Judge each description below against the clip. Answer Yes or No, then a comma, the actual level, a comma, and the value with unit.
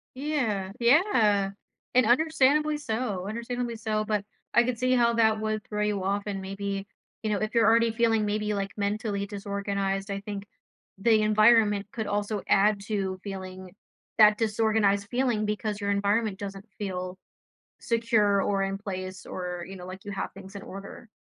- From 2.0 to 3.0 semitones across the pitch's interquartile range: Yes, narrow, 2.4 semitones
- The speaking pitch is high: Yes, high, 210 Hz